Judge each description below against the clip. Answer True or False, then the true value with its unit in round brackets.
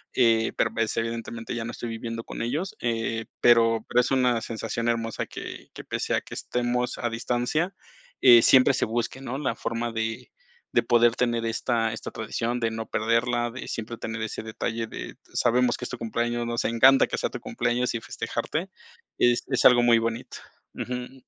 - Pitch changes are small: True (1.3 semitones)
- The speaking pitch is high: False (115 Hz)